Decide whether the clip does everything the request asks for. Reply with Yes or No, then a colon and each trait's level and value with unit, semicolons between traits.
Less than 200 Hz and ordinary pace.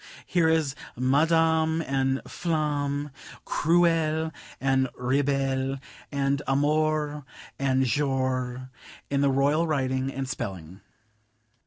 No: medium, 140 Hz; slow, 95 wpm